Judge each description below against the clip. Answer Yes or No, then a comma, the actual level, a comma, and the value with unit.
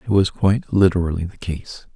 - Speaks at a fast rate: No, average, 185 wpm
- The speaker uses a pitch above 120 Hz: No, very low, 90 Hz